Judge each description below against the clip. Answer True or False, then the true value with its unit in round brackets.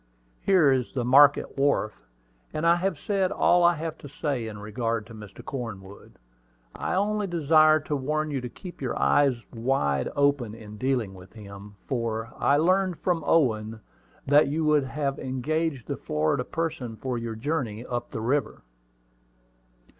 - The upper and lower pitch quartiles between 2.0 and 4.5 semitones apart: False (5.6 semitones)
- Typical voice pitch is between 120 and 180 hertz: True (135 Hz)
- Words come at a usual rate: True (160 wpm)